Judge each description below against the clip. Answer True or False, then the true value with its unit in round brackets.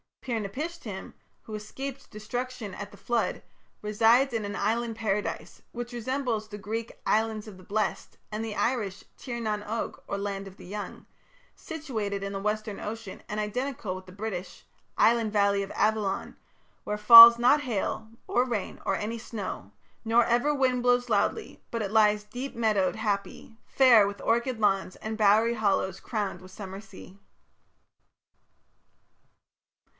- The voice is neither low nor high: False (215 Hz)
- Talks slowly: False (155 wpm)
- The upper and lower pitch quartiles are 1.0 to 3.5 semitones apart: True (2.8 semitones)